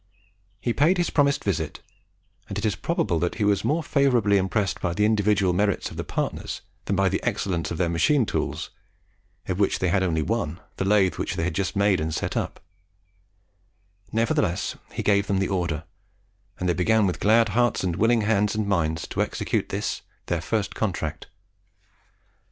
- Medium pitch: No, low, 100 Hz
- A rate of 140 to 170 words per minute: No, average, 185 wpm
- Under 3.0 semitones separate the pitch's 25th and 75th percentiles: No, average, 3.6 semitones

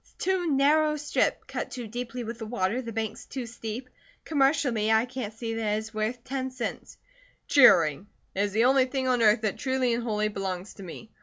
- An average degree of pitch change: Yes, average, 3.3 semitones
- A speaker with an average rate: No, fast, 215 wpm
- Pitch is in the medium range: No, high, 235 Hz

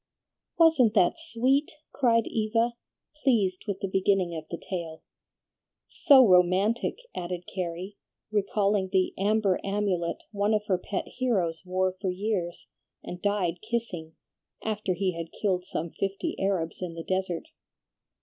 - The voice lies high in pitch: Yes, high, 195 Hz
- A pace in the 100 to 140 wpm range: Yes, slow, 135 wpm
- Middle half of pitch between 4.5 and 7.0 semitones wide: No, average, 3.2 semitones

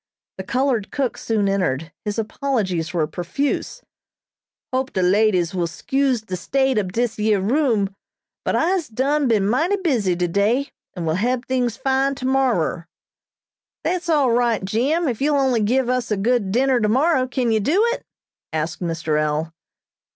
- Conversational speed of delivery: Yes, average, 160 wpm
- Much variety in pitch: Yes, wide, 5.9 semitones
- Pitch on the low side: No, high, 230 Hz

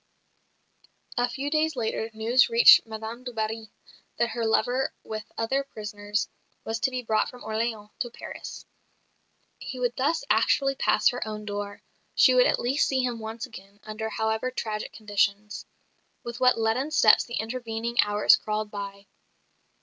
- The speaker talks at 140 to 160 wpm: Yes, average, 155 wpm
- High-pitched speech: Yes, high, 225 Hz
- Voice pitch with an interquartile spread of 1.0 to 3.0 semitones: Yes, narrow, 2.6 semitones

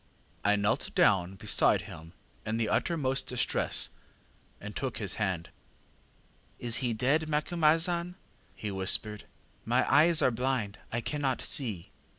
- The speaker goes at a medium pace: No, slow, 130 wpm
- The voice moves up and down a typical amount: No, wide, 6.2 semitones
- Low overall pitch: Yes, low, 120 Hz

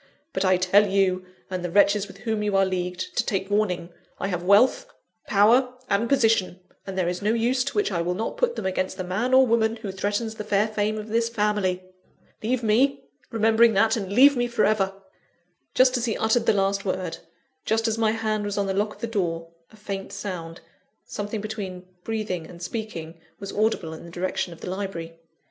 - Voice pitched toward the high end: Yes, high, 205 Hz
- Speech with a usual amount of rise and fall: Yes, average, 3.1 semitones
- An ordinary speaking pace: No, fast, 210 wpm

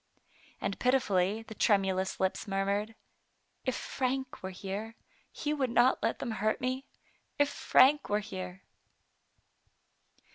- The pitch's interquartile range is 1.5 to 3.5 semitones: No, average, 4.8 semitones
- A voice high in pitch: Yes, high, 215 Hz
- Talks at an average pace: No, slow, 130 wpm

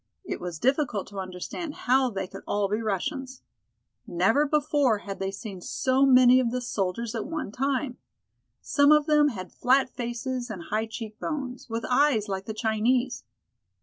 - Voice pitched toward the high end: Yes, high, 240 Hz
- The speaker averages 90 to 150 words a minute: No, average, 170 wpm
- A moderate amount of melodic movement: Yes, average, 4.6 semitones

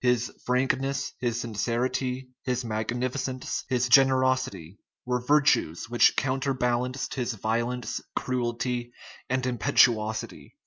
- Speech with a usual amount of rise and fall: No, narrow, 1.7 semitones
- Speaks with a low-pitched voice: Yes, low, 125 Hz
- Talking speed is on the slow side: Yes, slow, 95 wpm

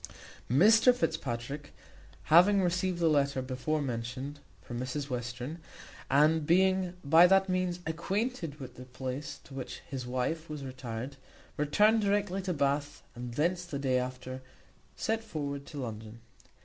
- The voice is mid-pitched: Yes, medium, 145 Hz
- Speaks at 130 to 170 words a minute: Yes, average, 140 wpm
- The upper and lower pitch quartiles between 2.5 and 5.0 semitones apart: No, wide, 5.6 semitones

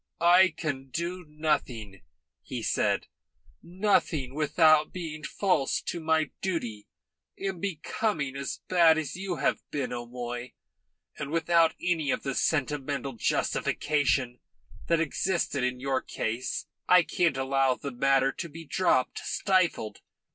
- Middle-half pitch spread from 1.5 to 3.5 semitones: No, average, 4.2 semitones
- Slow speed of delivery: Yes, slow, 125 wpm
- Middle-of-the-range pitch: Yes, medium, 150 Hz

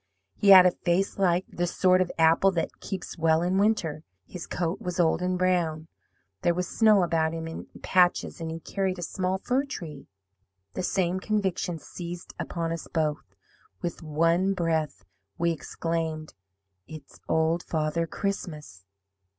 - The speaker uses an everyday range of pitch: No, narrow, 2.2 semitones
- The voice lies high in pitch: No, medium, 170 Hz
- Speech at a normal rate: Yes, average, 155 wpm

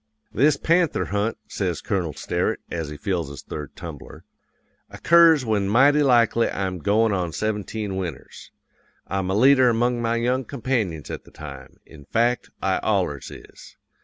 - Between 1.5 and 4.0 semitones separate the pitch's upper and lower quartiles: No, average, 5.2 semitones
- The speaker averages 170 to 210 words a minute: No, average, 155 wpm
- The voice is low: Yes, low, 110 Hz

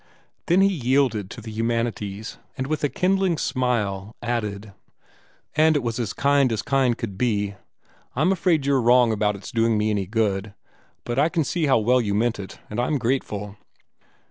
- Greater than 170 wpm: Yes, average, 180 wpm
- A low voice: Yes, low, 120 Hz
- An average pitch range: Yes, average, 4.7 semitones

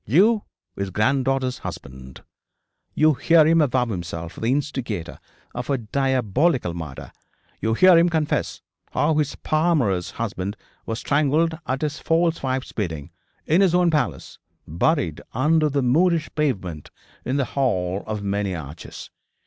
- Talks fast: No, average, 140 wpm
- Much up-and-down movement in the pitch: Yes, wide, 7.8 semitones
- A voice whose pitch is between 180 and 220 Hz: No, low, 130 Hz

